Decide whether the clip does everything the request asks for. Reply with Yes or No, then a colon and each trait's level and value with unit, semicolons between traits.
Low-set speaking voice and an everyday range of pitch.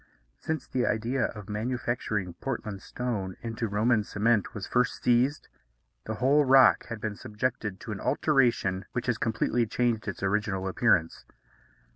Yes: low, 115 Hz; average, 3.1 semitones